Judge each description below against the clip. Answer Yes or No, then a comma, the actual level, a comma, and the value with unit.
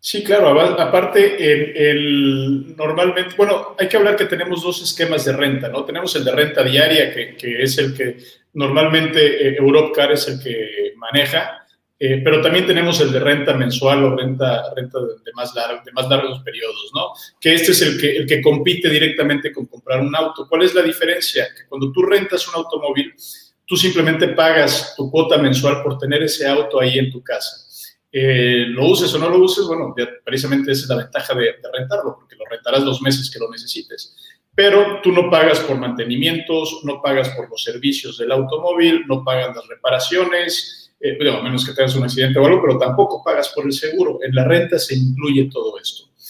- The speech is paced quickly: Yes, fast, 200 wpm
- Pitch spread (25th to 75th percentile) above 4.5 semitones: Yes, average, 5.2 semitones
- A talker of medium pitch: Yes, medium, 150 Hz